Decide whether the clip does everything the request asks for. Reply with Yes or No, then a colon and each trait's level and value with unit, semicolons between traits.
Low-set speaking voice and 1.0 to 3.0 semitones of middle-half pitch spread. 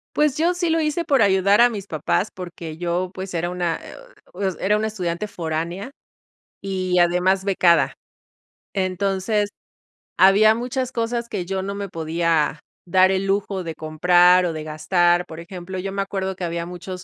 No: medium, 185 Hz; narrow, 2.6 semitones